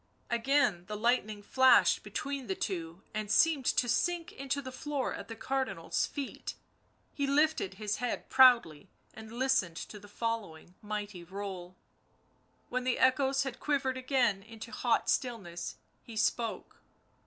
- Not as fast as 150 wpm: Yes, average, 140 wpm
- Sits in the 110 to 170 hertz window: No, high, 235 Hz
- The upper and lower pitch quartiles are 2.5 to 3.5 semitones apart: No, average, 4.6 semitones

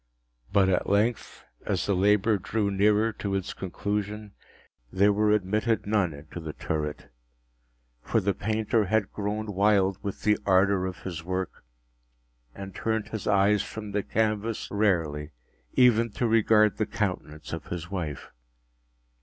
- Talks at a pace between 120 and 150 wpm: Yes, average, 140 wpm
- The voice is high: No, low, 100 Hz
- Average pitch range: No, narrow, 2.3 semitones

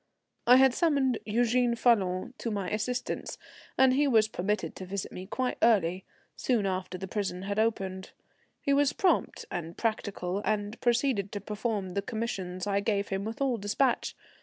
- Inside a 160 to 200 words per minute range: Yes, average, 165 wpm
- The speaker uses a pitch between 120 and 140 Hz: No, high, 210 Hz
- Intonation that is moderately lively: Yes, average, 4.0 semitones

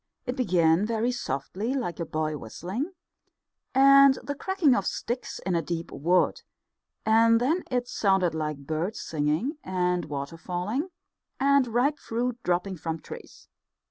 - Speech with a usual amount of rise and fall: No, wide, 7.2 semitones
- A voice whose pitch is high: Yes, high, 195 Hz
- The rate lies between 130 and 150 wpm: Yes, average, 140 wpm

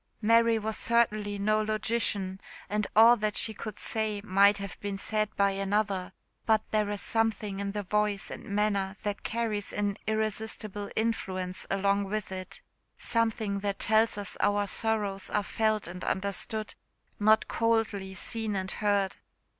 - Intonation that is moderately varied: No, narrow, 1.6 semitones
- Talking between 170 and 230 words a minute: No, average, 150 wpm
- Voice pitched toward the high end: Yes, high, 210 Hz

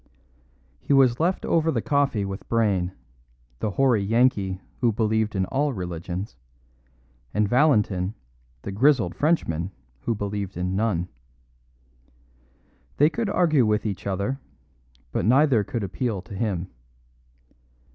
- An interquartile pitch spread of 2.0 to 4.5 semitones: No, wide, 5.6 semitones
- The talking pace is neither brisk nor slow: No, slow, 125 wpm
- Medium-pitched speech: No, low, 110 Hz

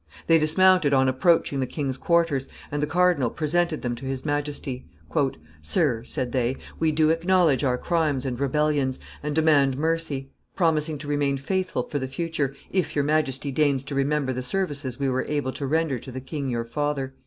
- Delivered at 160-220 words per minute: Yes, average, 185 wpm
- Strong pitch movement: No, average, 3.2 semitones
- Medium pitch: Yes, medium, 145 Hz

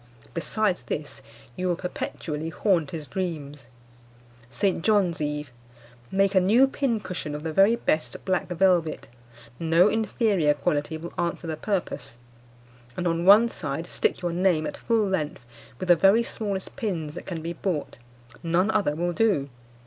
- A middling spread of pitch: Yes, average, 3.9 semitones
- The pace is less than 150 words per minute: No, average, 155 wpm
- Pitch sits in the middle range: Yes, medium, 175 Hz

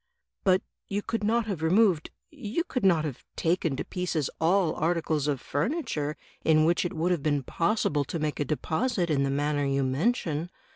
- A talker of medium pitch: Yes, medium, 160 Hz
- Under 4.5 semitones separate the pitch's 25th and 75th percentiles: No, average, 4.9 semitones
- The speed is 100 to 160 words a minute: No, average, 190 wpm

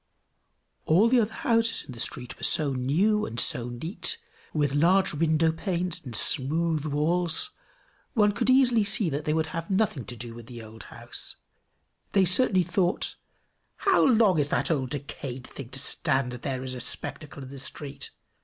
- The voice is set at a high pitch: No, medium, 155 Hz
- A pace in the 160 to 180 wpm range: Yes, average, 175 wpm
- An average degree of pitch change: No, wide, 6.4 semitones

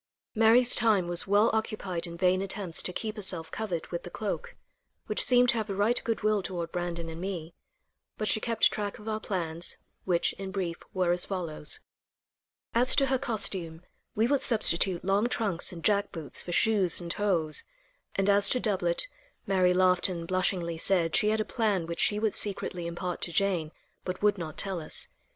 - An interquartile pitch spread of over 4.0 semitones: No, average, 3.7 semitones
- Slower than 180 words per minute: No, average, 190 wpm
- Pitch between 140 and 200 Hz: Yes, high, 190 Hz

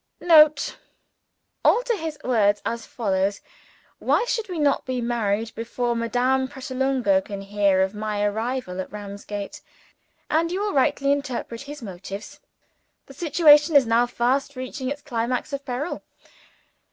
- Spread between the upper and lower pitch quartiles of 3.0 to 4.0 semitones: No, average, 5.3 semitones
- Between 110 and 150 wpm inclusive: Yes, average, 140 wpm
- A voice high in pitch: Yes, high, 245 Hz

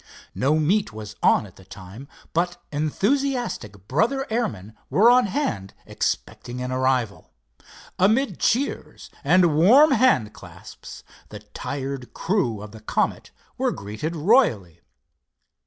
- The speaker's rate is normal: No, slow, 125 wpm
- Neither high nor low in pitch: Yes, medium, 150 Hz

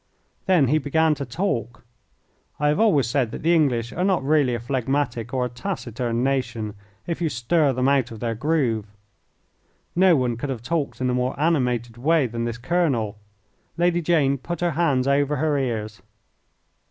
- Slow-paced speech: No, average, 175 wpm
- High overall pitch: No, low, 135 Hz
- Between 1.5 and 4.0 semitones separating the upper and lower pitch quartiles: No, average, 4.9 semitones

